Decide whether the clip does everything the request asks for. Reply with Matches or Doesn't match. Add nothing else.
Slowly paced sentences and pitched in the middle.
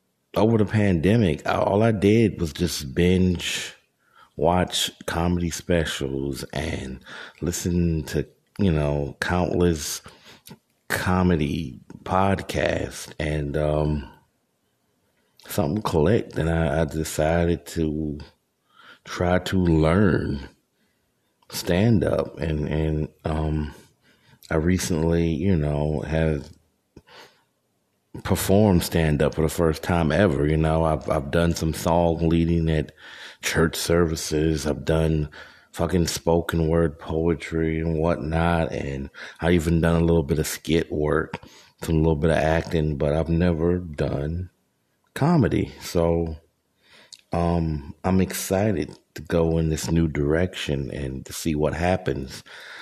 Doesn't match